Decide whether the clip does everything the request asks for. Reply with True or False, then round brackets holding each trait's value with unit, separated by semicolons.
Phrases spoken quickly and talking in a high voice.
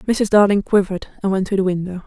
True (230 wpm; 195 Hz)